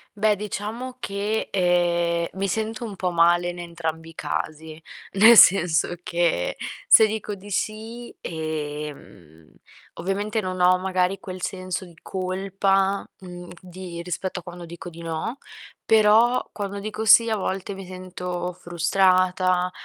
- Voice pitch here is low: No, medium, 185 Hz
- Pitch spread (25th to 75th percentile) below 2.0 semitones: No, average, 2.7 semitones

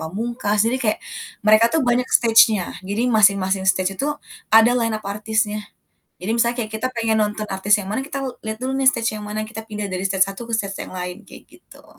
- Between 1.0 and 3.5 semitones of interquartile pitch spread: Yes, average, 2.7 semitones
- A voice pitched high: Yes, high, 215 Hz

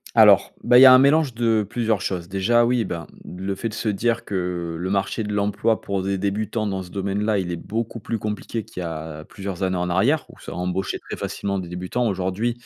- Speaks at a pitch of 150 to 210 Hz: No, low, 100 Hz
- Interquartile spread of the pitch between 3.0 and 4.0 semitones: Yes, average, 3.7 semitones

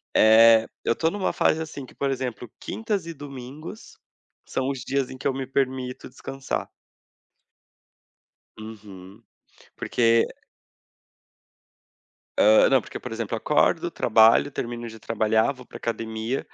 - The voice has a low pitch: Yes, low, 125 Hz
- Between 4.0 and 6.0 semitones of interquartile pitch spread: No, average, 3.5 semitones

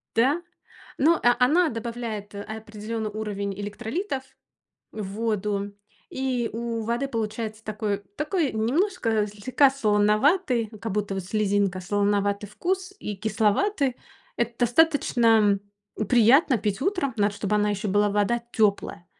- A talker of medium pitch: No, high, 220 Hz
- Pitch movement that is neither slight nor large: Yes, average, 3.6 semitones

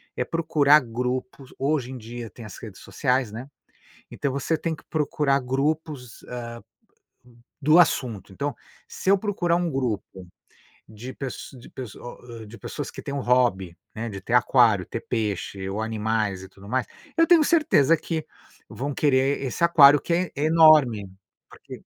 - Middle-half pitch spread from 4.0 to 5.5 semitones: Yes, average, 5.0 semitones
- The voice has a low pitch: Yes, low, 130 Hz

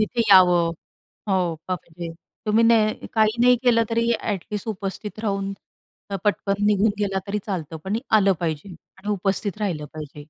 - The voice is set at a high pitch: Yes, high, 200 Hz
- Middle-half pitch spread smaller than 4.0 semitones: Yes, average, 3.2 semitones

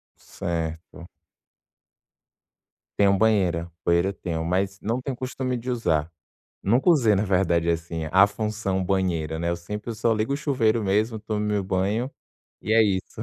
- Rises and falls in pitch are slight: No, average, 4.4 semitones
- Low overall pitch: Yes, low, 100 Hz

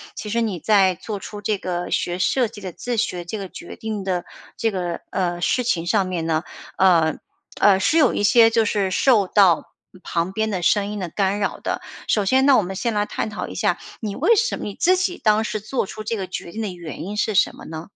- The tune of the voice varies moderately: Yes, average, 3.3 semitones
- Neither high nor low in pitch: No, high, 205 Hz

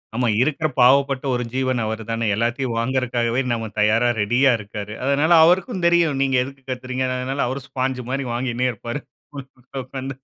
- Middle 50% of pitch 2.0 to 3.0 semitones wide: Yes, narrow, 2.5 semitones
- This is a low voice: Yes, low, 130 Hz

